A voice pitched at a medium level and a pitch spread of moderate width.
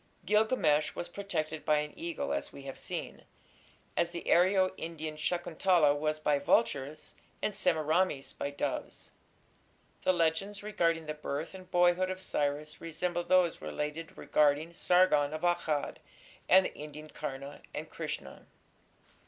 Yes: medium, 160 Hz; average, 3.2 semitones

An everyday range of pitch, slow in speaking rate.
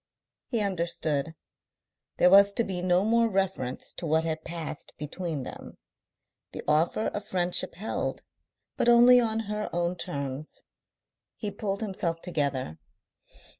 Yes: average, 4.4 semitones; slow, 130 wpm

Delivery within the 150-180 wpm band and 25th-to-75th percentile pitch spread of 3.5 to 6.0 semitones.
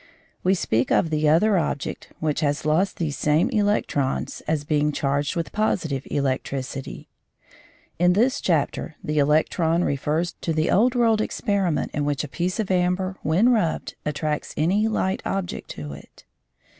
Yes: average, 155 wpm; average, 4.5 semitones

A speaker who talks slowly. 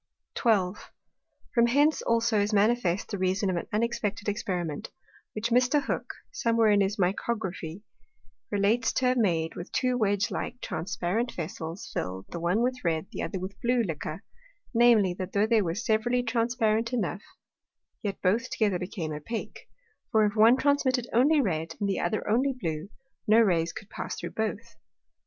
No: average, 170 wpm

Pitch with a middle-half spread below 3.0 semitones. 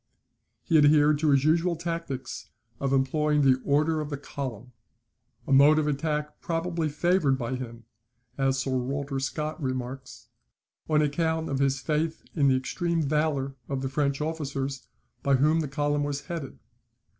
Yes: narrow, 2.5 semitones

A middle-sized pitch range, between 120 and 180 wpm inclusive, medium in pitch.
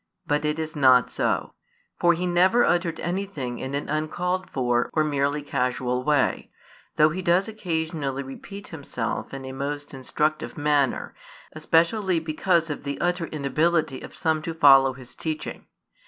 Yes: average, 3.8 semitones; average, 155 wpm; medium, 155 Hz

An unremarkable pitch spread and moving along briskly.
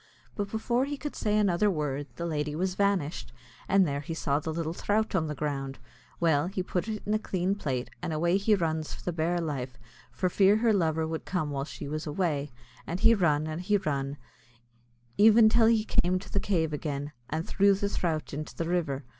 Yes: average, 4.9 semitones; fast, 215 wpm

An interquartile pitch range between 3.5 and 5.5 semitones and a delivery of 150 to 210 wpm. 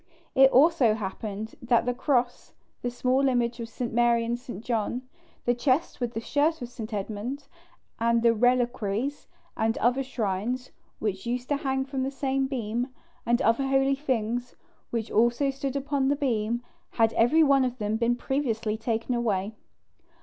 No: average, 2.9 semitones; average, 165 wpm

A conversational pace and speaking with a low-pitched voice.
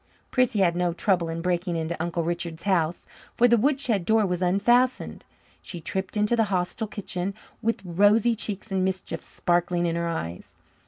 No: average, 170 wpm; medium, 185 Hz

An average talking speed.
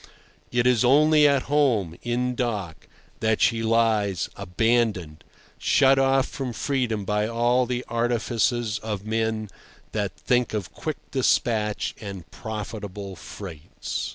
No: slow, 125 wpm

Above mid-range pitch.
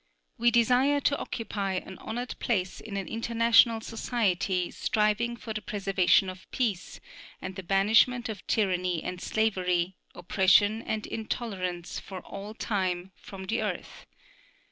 Yes: high, 205 Hz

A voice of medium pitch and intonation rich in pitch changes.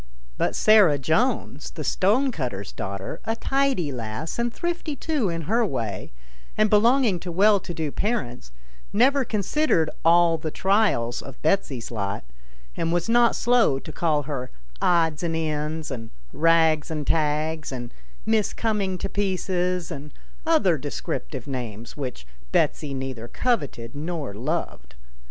Yes: medium, 160 Hz; wide, 7.7 semitones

